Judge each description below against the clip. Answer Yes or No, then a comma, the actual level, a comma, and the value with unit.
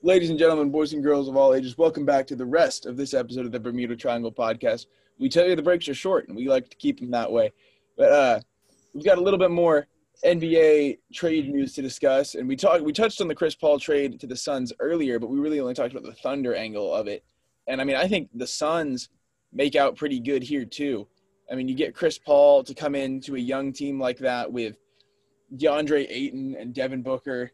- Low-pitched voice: No, medium, 145 Hz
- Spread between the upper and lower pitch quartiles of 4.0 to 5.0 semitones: Yes, average, 4.7 semitones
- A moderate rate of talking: No, fast, 235 wpm